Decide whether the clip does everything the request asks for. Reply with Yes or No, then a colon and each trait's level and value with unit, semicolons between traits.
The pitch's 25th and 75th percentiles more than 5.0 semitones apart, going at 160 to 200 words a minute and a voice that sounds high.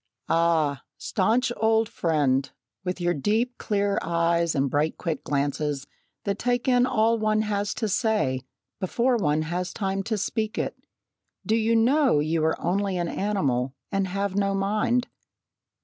No: wide, 5.4 semitones; average, 150 wpm; high, 195 Hz